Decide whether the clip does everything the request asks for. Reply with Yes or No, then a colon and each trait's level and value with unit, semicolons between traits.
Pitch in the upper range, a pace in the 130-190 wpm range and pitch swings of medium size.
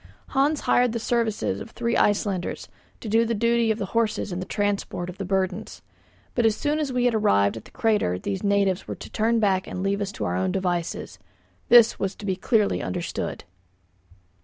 No: high, 205 Hz; fast, 205 wpm; average, 3.6 semitones